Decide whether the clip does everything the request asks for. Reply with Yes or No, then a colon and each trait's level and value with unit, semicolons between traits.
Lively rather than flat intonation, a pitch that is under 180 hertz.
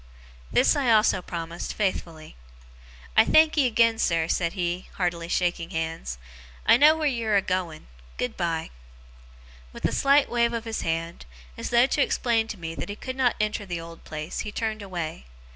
No: wide, 5.8 semitones; high, 190 Hz